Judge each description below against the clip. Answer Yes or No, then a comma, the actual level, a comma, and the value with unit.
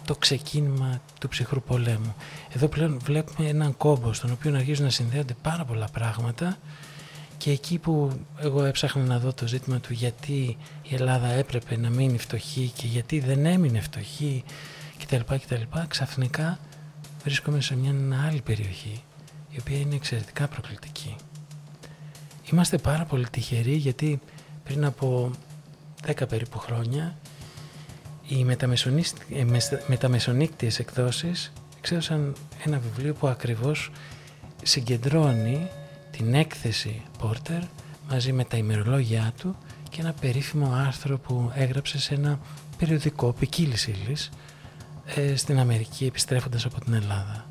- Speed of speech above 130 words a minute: No, average, 125 wpm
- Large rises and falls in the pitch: No, average, 3.3 semitones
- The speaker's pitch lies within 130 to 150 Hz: Yes, medium, 140 Hz